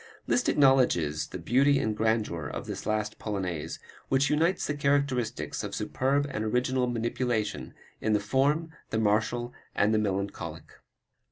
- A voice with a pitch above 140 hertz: No, low, 115 Hz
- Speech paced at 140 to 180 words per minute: Yes, average, 145 wpm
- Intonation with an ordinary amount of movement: Yes, average, 4.3 semitones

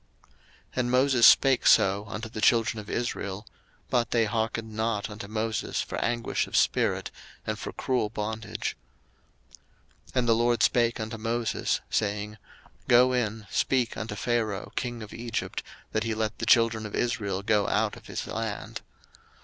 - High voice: No, low, 115 Hz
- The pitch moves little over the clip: Yes, narrow, 2.0 semitones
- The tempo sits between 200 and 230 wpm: No, average, 165 wpm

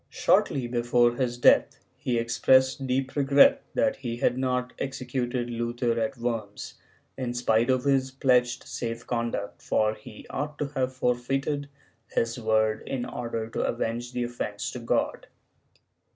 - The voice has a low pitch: Yes, low, 120 Hz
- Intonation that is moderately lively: No, narrow, 1.9 semitones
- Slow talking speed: No, average, 150 wpm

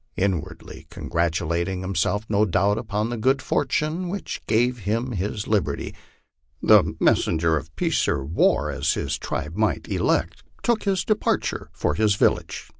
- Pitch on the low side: Yes, low, 105 Hz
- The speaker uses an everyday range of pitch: No, wide, 5.9 semitones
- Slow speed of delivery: No, average, 145 wpm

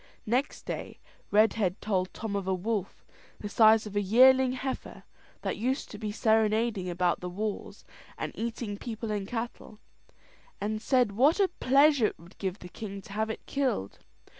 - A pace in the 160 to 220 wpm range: Yes, average, 170 wpm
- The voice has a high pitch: Yes, high, 215 Hz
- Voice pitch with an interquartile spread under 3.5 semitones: Yes, average, 3.1 semitones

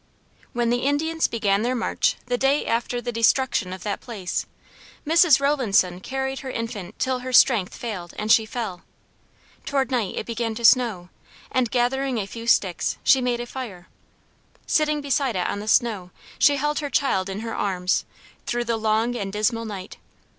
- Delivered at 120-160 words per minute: No, average, 175 wpm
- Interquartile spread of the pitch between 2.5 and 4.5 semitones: Yes, average, 4.1 semitones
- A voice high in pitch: Yes, high, 235 Hz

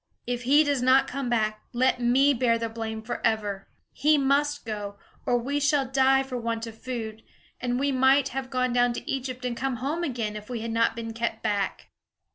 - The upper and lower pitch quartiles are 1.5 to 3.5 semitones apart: Yes, average, 2.9 semitones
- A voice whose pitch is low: No, high, 245 Hz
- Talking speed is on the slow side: No, fast, 205 wpm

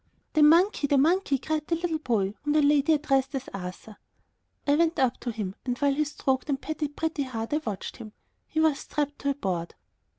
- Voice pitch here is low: No, very high, 285 Hz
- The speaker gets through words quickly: Yes, fast, 210 wpm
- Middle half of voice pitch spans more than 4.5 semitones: No, average, 3.8 semitones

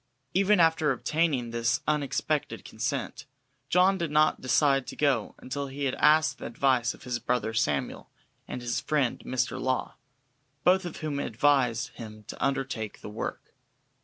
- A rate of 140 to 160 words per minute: Yes, average, 155 wpm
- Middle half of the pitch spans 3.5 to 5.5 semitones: Yes, average, 4.1 semitones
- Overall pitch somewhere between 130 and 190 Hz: Yes, low, 135 Hz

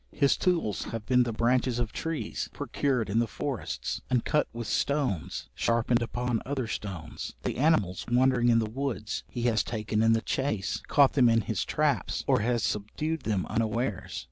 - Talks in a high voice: No, low, 120 Hz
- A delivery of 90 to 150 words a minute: No, average, 175 wpm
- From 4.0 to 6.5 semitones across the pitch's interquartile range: No, average, 3.1 semitones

